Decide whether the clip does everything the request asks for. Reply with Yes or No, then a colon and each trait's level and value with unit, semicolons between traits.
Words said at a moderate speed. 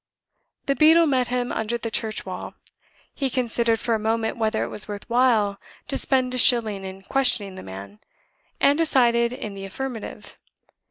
Yes: average, 170 wpm